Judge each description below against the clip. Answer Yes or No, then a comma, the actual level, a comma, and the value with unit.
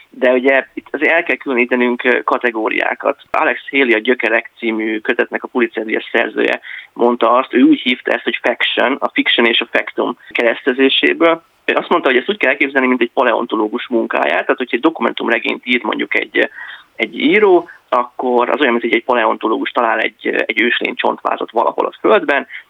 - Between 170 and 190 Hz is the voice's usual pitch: No, low, 125 Hz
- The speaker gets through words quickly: Yes, fast, 175 wpm